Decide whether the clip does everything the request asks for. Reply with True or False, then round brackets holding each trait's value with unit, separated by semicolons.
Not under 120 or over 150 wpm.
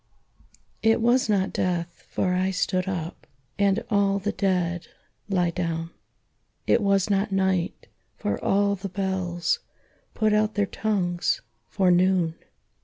True (135 wpm)